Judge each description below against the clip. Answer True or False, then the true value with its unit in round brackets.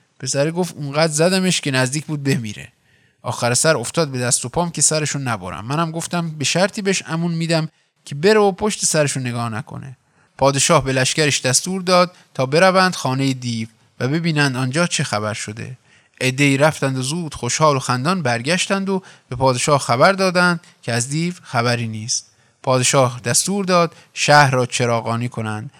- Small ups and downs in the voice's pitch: False (5.1 semitones)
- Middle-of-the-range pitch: True (145 Hz)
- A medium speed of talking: False (165 wpm)